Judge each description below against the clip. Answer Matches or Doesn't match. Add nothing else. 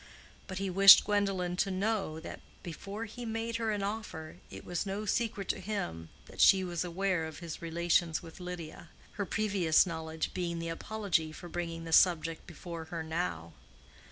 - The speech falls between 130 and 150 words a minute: Doesn't match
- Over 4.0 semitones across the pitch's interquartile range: Doesn't match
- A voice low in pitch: Doesn't match